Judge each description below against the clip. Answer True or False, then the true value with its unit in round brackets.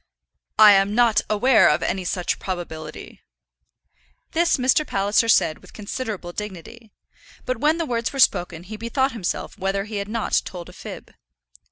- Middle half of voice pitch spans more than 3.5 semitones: True (4.2 semitones)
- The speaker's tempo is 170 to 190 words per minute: False (160 wpm)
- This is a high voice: True (210 Hz)